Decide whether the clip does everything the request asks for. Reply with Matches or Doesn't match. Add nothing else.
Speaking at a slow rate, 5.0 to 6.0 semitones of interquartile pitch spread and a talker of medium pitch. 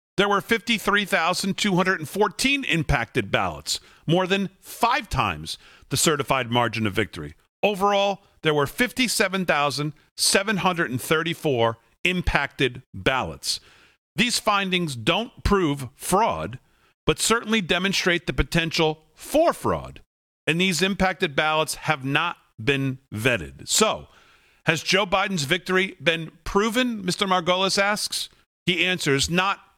Matches